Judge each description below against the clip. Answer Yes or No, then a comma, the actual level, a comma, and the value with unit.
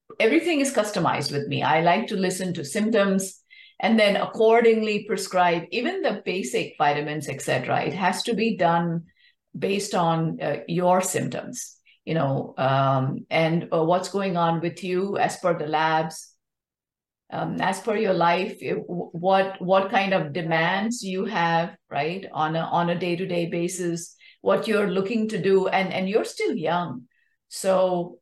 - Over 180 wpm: No, average, 155 wpm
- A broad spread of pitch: No, average, 3.3 semitones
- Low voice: No, medium, 185 Hz